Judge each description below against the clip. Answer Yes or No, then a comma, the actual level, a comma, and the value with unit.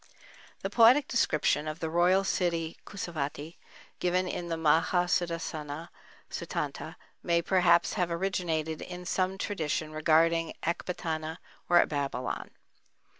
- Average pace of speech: No, slow, 115 wpm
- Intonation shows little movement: Yes, narrow, 2.3 semitones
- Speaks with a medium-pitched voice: Yes, medium, 170 Hz